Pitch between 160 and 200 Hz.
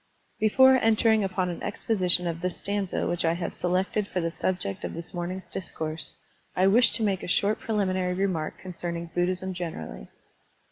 Yes: medium, 185 Hz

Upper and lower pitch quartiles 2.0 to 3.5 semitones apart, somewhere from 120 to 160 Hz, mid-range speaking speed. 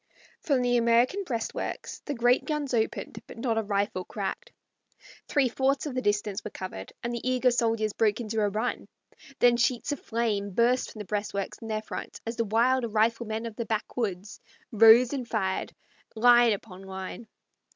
No: average, 2.7 semitones; high, 230 Hz; average, 175 wpm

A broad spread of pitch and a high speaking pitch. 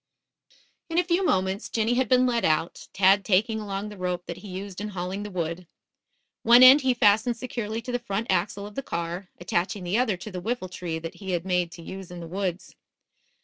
No: average, 4.3 semitones; high, 200 Hz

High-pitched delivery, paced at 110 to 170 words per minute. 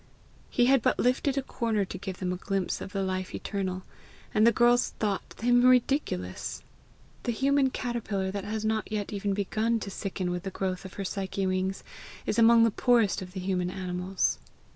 No: high, 200 Hz; average, 190 wpm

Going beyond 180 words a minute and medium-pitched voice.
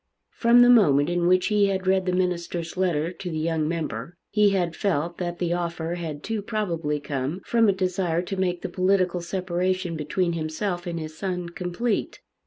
Yes: average, 190 wpm; medium, 175 Hz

